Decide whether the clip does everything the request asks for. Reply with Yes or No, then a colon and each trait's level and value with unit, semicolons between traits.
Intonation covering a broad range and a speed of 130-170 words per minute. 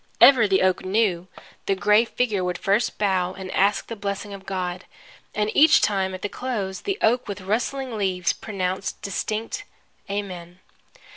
No: average, 2.7 semitones; average, 160 wpm